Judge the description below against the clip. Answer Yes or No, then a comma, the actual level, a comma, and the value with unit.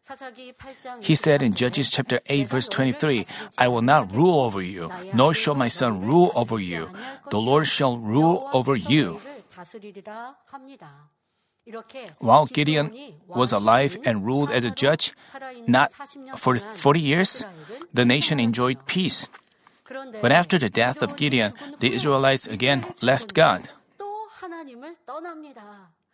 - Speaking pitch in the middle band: Yes, medium, 155 Hz